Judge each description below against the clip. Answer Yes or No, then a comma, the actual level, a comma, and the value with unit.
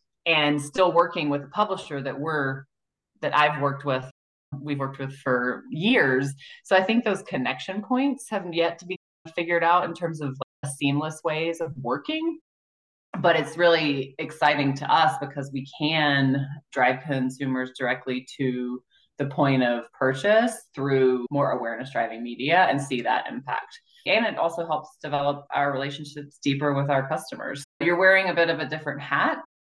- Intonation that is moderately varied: Yes, average, 3.8 semitones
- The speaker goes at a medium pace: Yes, average, 165 wpm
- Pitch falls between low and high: Yes, medium, 145 Hz